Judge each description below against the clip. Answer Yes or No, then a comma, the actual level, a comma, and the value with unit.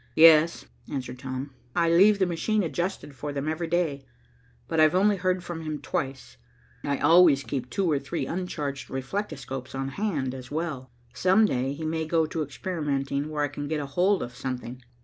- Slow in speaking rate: No, average, 180 wpm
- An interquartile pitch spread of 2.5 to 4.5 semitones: Yes, average, 4.1 semitones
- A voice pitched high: No, medium, 155 Hz